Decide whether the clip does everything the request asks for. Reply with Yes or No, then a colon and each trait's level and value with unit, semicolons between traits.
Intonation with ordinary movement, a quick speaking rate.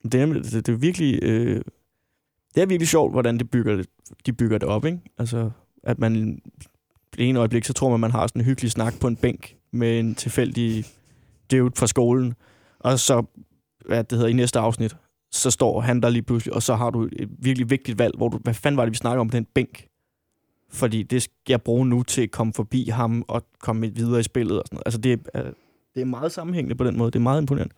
No: narrow, 1.9 semitones; fast, 245 wpm